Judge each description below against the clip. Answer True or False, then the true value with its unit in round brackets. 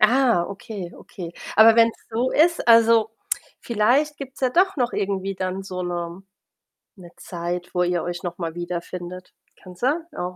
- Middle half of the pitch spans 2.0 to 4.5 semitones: False (5.0 semitones)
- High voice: True (195 Hz)